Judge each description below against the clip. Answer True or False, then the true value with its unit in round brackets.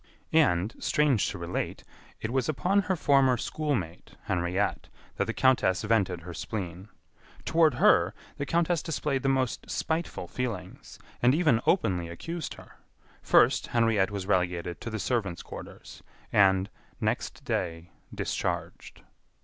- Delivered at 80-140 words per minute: True (135 wpm)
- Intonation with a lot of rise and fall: True (7.5 semitones)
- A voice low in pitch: True (110 Hz)